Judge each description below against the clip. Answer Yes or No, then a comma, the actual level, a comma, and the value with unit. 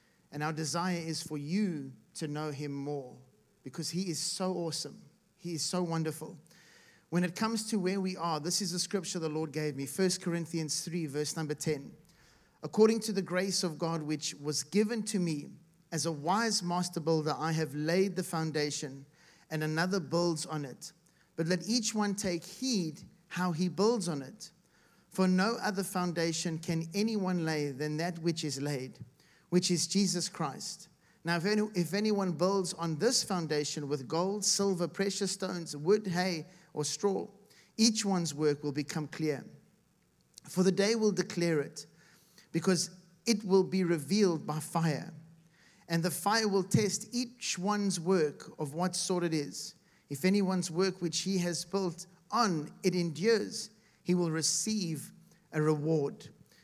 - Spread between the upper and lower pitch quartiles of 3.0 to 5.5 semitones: Yes, average, 3.4 semitones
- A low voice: No, medium, 175 Hz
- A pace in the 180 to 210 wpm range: No, average, 165 wpm